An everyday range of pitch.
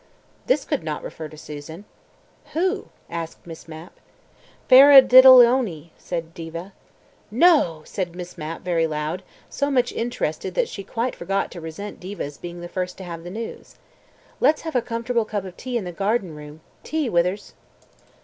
No: wide, 6.7 semitones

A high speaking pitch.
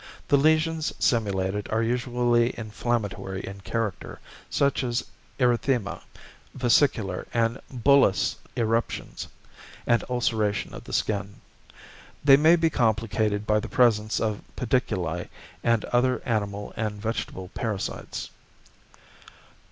No: low, 115 Hz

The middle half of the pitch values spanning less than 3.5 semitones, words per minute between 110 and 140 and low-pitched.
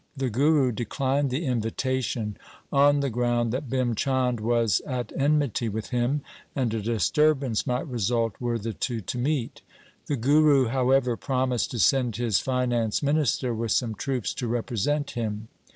No: average, 2.9 semitones; average, 160 wpm; low, 125 Hz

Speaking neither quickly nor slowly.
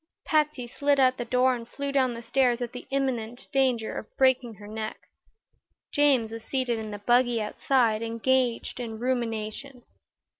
Yes: average, 160 wpm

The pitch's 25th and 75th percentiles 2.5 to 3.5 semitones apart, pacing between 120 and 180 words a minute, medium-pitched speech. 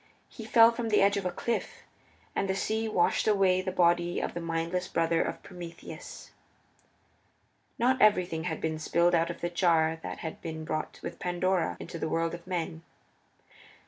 Yes: average, 2.8 semitones; average, 175 wpm; medium, 175 Hz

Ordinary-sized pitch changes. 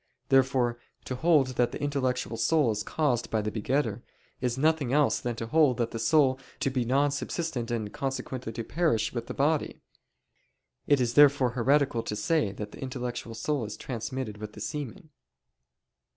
Yes: average, 3.7 semitones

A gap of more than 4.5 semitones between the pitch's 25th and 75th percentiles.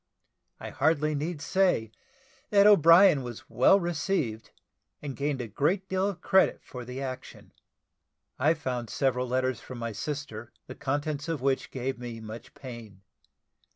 Yes: average, 4.9 semitones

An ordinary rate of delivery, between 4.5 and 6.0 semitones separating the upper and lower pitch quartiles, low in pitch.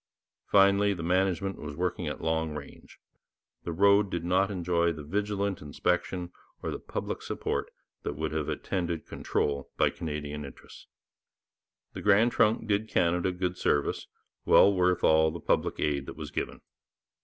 No: average, 155 wpm; average, 3.9 semitones; very low, 90 Hz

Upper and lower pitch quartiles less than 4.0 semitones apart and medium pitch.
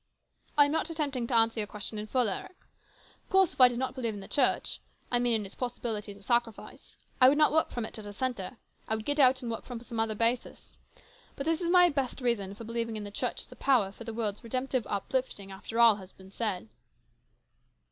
No: average, 3.5 semitones; high, 235 Hz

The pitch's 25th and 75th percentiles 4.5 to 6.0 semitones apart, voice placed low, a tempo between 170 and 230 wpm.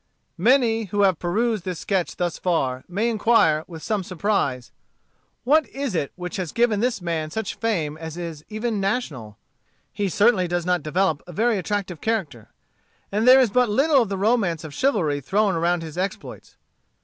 No: average, 5.2 semitones; high, 190 Hz; average, 175 wpm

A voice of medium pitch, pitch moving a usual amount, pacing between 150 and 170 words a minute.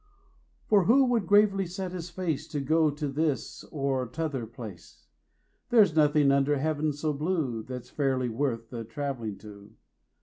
Yes: medium, 145 Hz; average, 4.4 semitones; average, 160 wpm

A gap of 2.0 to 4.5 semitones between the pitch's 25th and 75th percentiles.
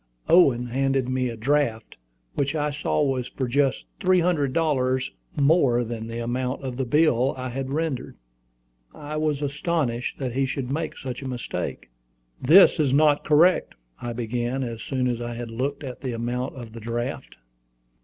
Yes: average, 3.3 semitones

